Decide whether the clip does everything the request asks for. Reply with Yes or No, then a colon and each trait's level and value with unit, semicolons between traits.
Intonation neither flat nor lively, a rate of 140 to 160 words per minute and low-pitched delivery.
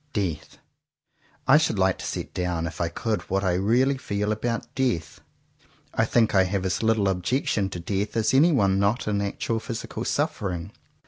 No: average, 3.6 semitones; average, 175 wpm; low, 100 Hz